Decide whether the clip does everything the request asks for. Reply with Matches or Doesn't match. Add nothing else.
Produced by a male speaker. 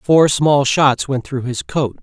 Matches